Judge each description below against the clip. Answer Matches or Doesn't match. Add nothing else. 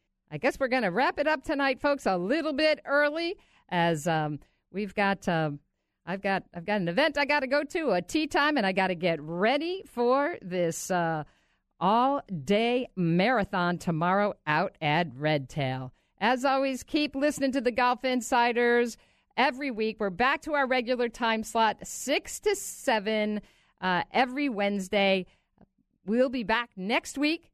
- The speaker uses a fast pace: Doesn't match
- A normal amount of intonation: Doesn't match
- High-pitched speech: Matches